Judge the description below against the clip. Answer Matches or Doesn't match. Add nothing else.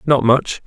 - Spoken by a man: Matches